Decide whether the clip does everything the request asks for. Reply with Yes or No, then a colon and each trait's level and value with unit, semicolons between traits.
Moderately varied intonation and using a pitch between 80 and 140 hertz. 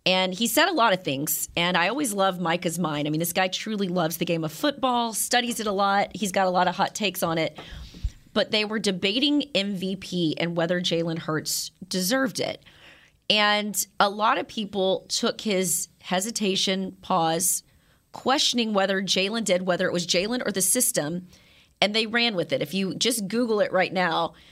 No: average, 3.7 semitones; high, 190 Hz